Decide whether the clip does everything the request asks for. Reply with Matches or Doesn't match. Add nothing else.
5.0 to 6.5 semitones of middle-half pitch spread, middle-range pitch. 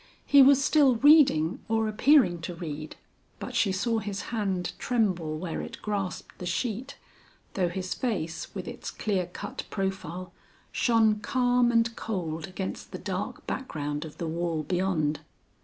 Doesn't match